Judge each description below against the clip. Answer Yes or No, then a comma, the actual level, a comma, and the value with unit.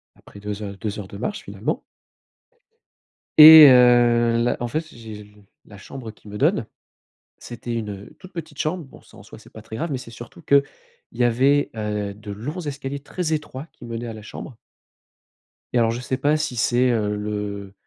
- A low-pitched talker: Yes, low, 120 Hz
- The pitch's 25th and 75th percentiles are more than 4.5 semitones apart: Yes, average, 5.0 semitones